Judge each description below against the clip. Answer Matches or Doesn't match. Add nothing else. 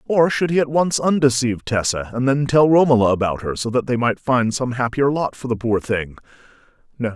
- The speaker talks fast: Matches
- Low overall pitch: Matches